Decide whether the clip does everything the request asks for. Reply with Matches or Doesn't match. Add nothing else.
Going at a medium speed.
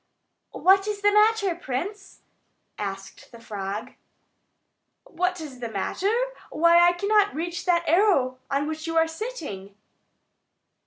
Doesn't match